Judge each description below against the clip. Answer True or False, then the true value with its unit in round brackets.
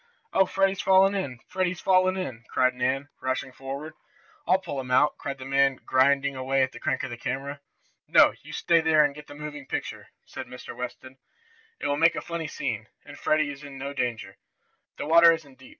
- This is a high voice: False (140 Hz)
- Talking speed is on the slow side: False (205 wpm)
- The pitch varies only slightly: False (3.6 semitones)